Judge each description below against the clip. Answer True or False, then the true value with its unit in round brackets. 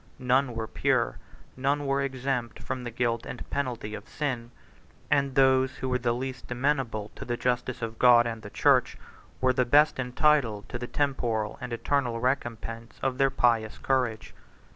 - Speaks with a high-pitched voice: False (125 Hz)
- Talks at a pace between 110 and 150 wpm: False (170 wpm)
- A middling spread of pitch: False (2.3 semitones)